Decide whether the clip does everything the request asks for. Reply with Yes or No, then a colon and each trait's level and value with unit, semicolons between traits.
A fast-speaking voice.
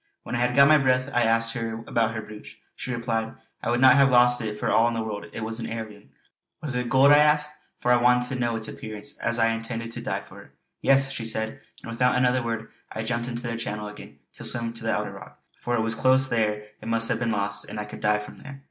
Yes: fast, 265 wpm